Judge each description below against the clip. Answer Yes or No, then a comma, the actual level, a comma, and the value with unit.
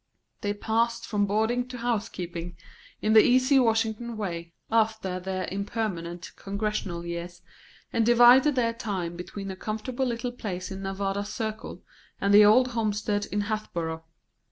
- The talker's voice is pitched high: Yes, high, 210 Hz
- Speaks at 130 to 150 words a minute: Yes, average, 145 wpm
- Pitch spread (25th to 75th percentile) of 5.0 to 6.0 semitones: No, average, 3.4 semitones